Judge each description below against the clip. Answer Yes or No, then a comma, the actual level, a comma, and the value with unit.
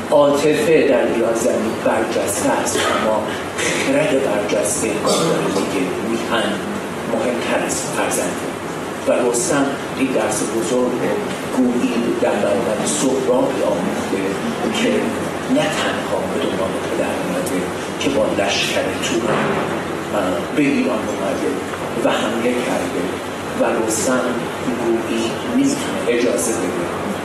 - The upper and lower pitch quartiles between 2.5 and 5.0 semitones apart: Yes, average, 4.7 semitones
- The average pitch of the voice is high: No, low, 125 Hz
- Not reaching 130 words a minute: Yes, average, 110 wpm